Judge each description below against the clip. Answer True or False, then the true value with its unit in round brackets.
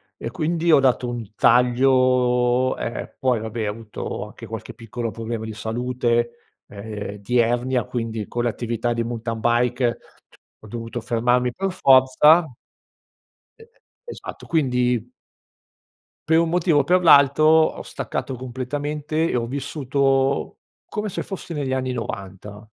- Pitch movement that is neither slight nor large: True (3.2 semitones)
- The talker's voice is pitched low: True (125 Hz)